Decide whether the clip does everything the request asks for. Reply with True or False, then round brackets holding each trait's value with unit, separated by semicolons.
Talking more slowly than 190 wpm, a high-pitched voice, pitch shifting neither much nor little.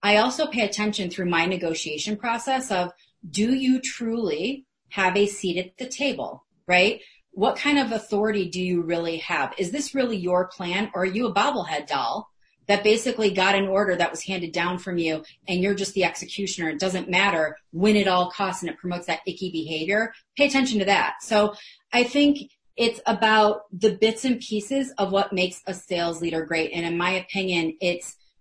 False (195 wpm; 195 Hz; 3.6 semitones)